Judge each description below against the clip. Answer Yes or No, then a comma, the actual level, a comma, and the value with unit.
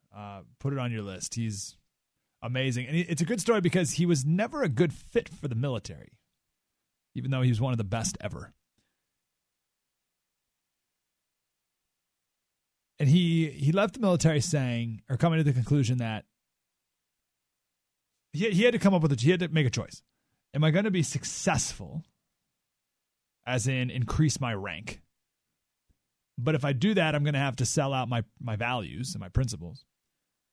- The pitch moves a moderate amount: No, wide, 7.7 semitones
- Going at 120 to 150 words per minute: No, average, 175 wpm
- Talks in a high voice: No, low, 130 Hz